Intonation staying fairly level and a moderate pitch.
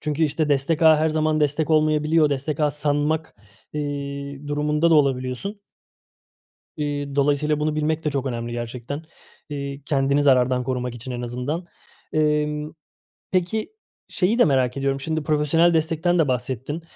Yes: narrow, 2.2 semitones; medium, 150 Hz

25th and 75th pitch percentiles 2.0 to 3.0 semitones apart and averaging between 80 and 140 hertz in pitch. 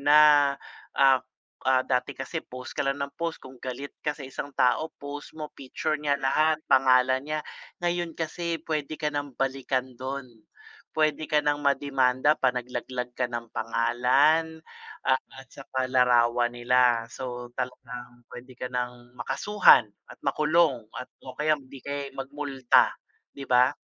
Yes: average, 2.7 semitones; low, 135 Hz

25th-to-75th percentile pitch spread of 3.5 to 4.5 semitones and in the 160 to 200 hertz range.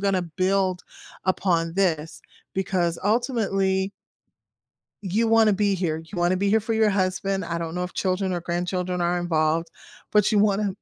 No: narrow, 2.4 semitones; medium, 185 Hz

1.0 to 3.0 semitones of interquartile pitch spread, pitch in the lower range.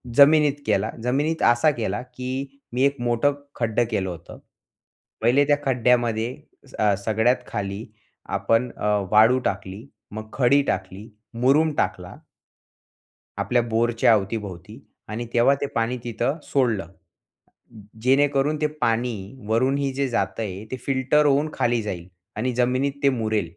No: average, 3.9 semitones; low, 120 Hz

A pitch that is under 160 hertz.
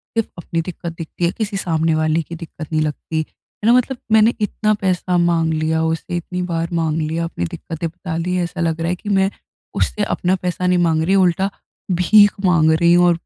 No: medium, 170 Hz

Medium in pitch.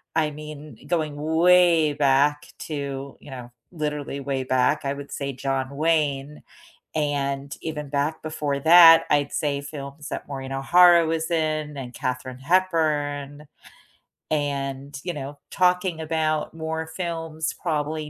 Yes: medium, 150 Hz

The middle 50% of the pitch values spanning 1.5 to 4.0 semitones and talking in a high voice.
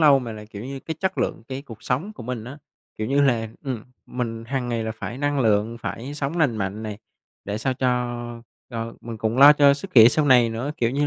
No: average, 3.6 semitones; low, 125 Hz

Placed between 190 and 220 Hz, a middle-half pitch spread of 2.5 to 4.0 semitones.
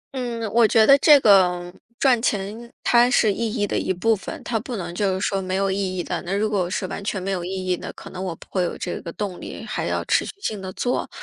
Yes: high, 195 Hz; average, 3.5 semitones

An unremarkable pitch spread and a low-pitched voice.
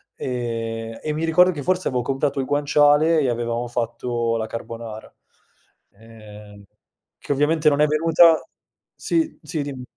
Yes: average, 4.7 semitones; low, 130 Hz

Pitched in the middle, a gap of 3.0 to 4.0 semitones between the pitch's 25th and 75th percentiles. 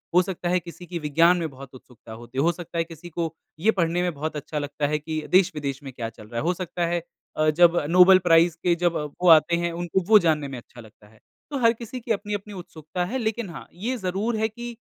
Yes: medium, 170 Hz; average, 3.5 semitones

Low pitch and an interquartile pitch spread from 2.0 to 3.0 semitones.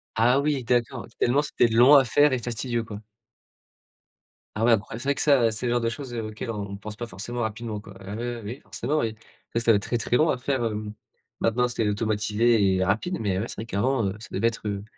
Yes: low, 115 Hz; narrow, 2.5 semitones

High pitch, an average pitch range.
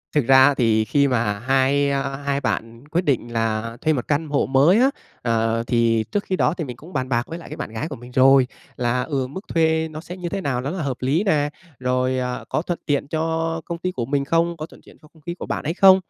No: medium, 140 Hz; average, 4.5 semitones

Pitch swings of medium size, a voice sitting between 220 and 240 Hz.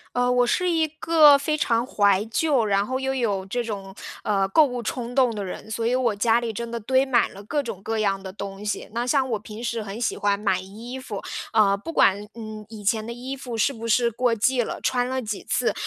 Yes: average, 3.6 semitones; high, 230 Hz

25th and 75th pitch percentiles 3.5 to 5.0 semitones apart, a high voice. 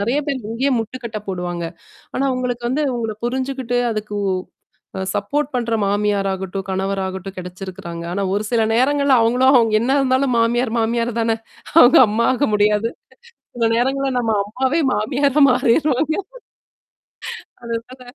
Yes: average, 4.0 semitones; high, 235 Hz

